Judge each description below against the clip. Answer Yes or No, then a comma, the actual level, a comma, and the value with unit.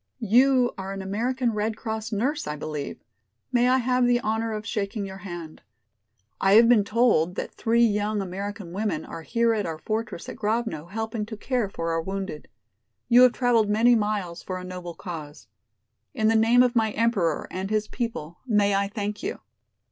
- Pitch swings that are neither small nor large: Yes, average, 3.5 semitones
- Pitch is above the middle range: Yes, high, 215 Hz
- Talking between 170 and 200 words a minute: Yes, average, 185 wpm